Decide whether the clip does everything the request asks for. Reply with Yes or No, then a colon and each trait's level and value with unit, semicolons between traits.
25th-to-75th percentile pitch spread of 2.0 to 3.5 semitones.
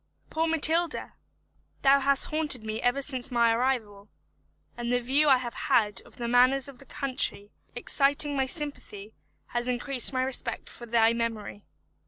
Yes: average, 3.0 semitones